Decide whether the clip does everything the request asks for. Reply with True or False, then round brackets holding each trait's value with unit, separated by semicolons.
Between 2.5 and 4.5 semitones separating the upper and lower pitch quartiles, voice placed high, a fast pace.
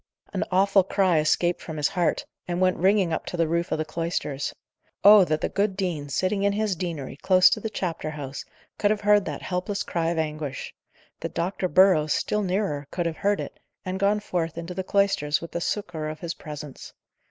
False (4.0 semitones; 175 Hz; 210 wpm)